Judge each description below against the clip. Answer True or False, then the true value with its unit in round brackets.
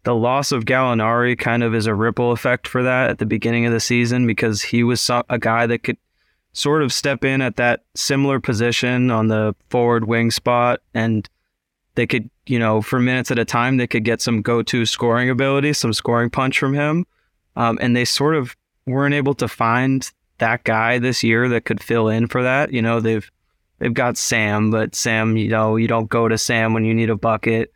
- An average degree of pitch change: False (1.9 semitones)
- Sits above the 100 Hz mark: True (120 Hz)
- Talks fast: True (215 wpm)